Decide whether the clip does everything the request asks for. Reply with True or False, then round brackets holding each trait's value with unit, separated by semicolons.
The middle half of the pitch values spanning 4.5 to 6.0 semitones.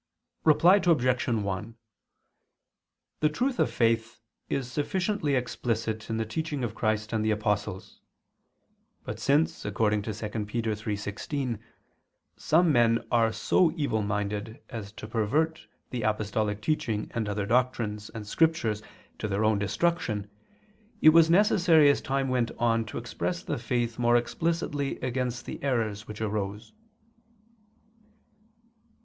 True (4.8 semitones)